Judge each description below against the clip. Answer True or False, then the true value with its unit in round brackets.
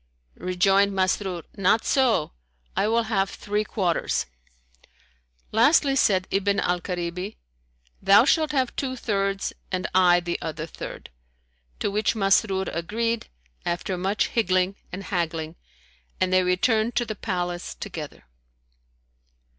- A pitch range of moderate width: True (3.3 semitones)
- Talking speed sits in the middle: False (125 wpm)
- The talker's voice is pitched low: False (195 Hz)